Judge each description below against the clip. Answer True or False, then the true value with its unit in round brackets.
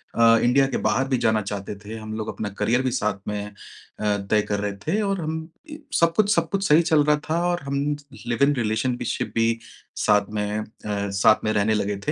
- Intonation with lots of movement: True (6.2 semitones)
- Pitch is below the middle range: True (115 Hz)